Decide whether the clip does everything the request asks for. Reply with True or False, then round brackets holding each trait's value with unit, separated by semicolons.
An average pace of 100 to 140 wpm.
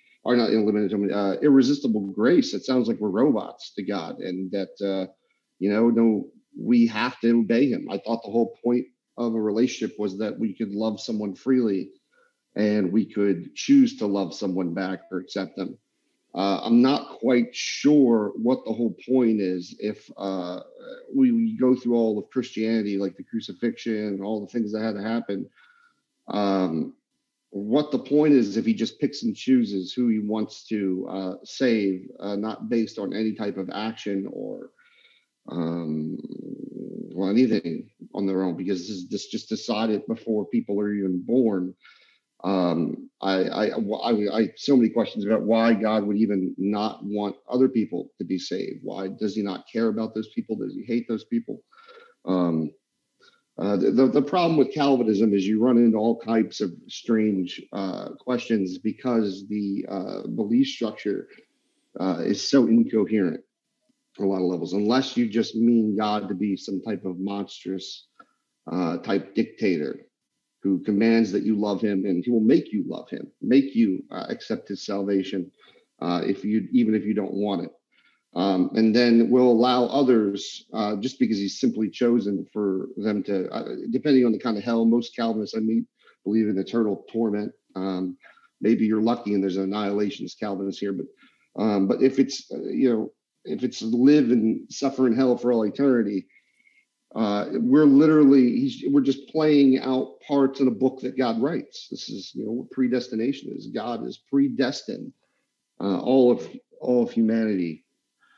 False (175 wpm)